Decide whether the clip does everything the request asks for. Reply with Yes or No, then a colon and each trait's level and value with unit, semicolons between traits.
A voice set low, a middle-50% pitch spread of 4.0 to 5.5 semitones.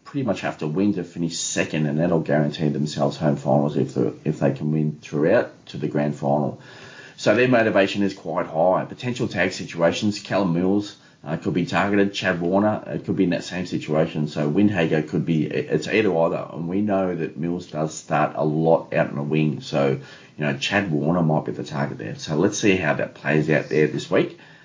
Yes: very low, 80 Hz; average, 4.6 semitones